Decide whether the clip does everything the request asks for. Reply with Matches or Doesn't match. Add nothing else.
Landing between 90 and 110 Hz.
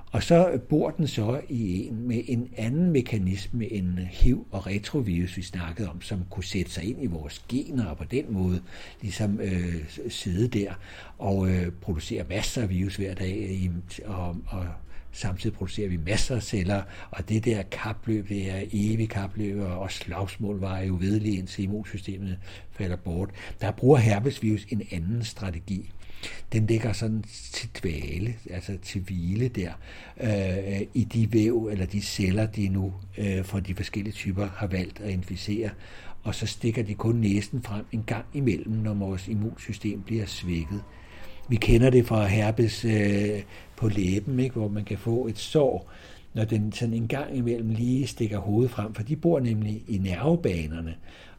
Matches